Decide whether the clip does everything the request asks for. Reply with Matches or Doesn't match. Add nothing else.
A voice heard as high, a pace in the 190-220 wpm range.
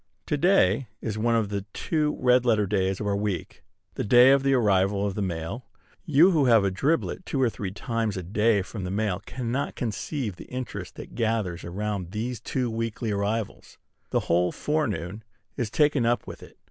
Doesn't match